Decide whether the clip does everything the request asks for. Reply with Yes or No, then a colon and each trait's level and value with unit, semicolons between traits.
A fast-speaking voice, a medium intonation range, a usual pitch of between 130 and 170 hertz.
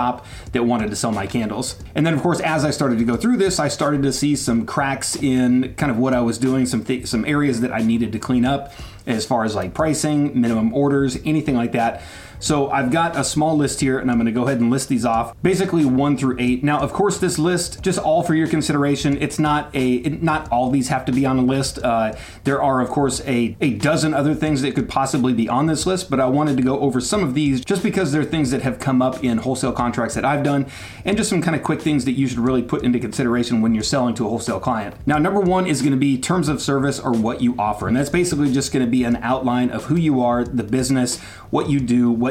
Yes: fast, 265 wpm; average, 3.5 semitones; low, 135 Hz